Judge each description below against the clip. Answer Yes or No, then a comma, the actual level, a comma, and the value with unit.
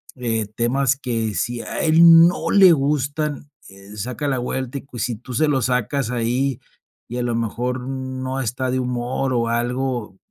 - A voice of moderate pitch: No, low, 125 Hz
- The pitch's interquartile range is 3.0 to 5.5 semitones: No, narrow, 2.4 semitones